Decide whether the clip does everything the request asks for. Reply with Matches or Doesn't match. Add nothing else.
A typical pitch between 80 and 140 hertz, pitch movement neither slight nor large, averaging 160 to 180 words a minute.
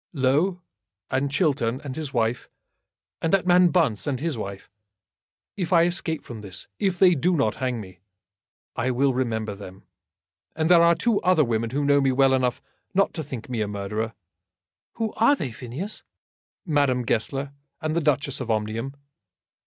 Doesn't match